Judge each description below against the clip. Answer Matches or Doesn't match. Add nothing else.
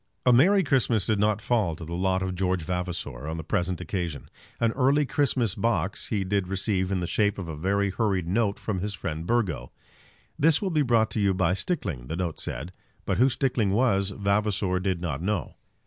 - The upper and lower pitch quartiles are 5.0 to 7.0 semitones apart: Doesn't match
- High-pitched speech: Doesn't match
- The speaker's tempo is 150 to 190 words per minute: Doesn't match